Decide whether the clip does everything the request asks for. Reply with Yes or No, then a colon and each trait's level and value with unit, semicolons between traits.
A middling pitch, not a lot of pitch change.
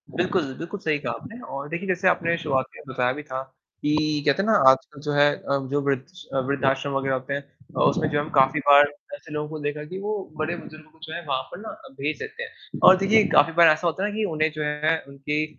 No: medium, 155 Hz; average, 3.7 semitones